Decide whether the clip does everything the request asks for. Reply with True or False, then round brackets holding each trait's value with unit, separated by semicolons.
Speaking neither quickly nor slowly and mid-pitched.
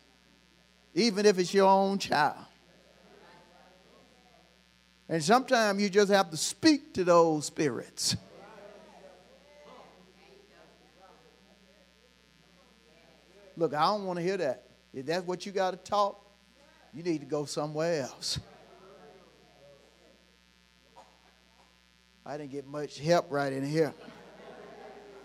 False (105 wpm; 175 Hz)